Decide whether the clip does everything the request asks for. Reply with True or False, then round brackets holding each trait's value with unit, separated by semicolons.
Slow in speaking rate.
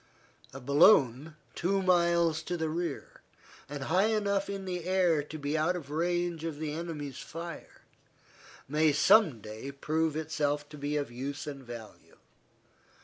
False (150 wpm)